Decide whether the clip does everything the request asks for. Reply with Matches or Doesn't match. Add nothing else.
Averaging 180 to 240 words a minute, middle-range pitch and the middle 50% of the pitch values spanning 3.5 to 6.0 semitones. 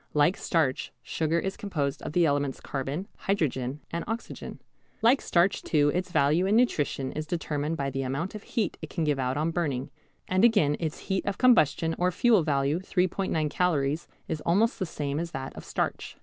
Matches